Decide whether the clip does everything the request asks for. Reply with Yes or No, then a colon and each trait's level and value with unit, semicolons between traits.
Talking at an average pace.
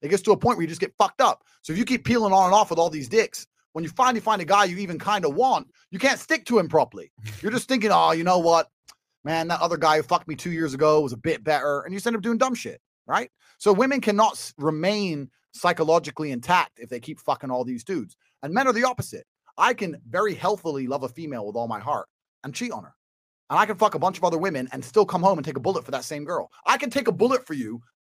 No: fast, 280 wpm